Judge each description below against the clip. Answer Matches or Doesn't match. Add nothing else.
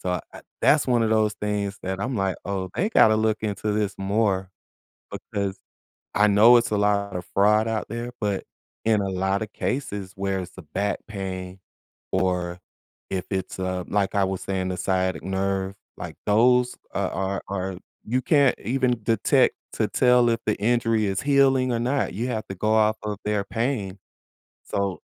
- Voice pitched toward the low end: Matches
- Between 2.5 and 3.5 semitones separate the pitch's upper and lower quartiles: Matches